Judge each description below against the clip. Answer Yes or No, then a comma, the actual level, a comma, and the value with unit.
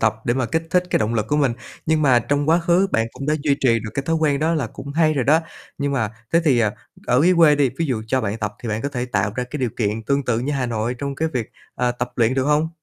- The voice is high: No, low, 135 Hz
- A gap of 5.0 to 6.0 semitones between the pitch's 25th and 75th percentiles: No, average, 4.4 semitones